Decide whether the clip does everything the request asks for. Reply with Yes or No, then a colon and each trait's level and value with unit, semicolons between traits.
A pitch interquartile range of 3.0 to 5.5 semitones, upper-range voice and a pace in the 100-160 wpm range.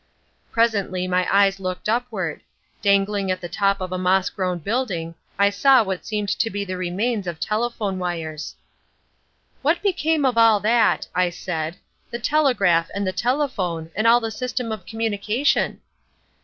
Yes: average, 4.0 semitones; high, 200 Hz; average, 155 wpm